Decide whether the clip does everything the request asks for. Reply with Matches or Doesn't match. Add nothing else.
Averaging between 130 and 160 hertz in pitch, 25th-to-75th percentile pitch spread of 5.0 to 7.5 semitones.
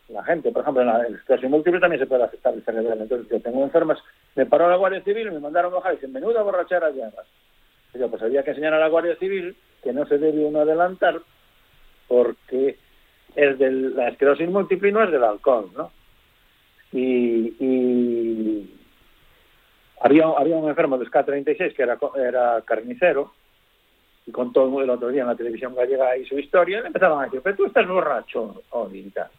Matches